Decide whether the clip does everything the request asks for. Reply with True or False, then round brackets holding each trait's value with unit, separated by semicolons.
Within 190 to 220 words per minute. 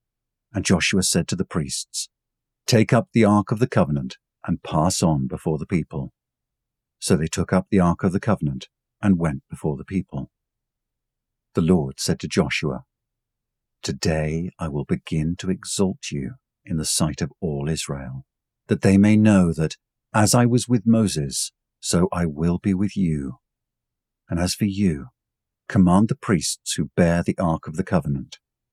False (170 wpm)